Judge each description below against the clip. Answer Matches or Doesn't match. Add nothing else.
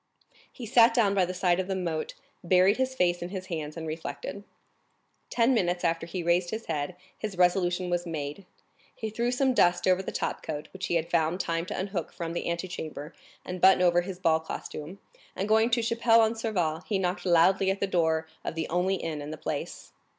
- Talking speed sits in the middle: Doesn't match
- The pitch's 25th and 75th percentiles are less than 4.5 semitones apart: Matches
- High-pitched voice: Doesn't match